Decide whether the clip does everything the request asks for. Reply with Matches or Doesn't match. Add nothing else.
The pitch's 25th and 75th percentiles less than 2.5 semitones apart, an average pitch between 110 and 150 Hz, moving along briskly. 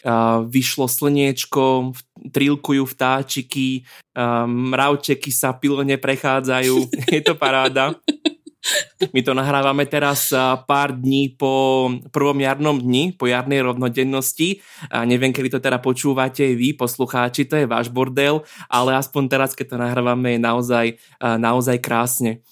Doesn't match